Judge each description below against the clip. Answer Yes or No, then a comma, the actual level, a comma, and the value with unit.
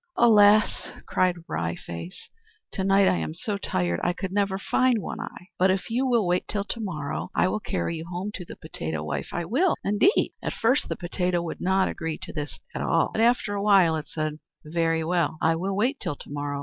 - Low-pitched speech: No, medium, 180 Hz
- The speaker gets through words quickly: Yes, fast, 225 wpm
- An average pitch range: Yes, average, 4.3 semitones